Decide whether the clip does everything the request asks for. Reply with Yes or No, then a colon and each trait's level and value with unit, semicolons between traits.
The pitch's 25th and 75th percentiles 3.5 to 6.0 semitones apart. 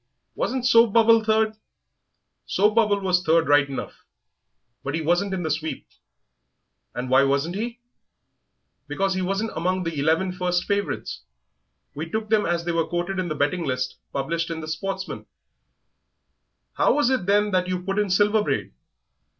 Yes: average, 4.4 semitones